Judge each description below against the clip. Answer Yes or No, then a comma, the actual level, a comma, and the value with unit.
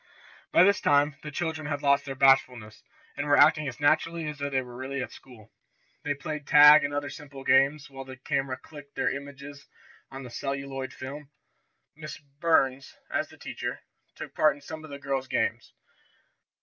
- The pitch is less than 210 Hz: Yes, medium, 140 Hz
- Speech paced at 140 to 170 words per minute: No, average, 185 wpm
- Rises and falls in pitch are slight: Yes, narrow, 1.6 semitones